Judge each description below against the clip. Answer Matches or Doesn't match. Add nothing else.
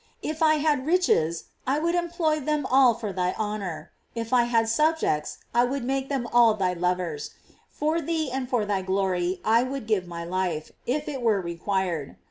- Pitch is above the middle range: Matches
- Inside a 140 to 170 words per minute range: Doesn't match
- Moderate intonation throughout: Doesn't match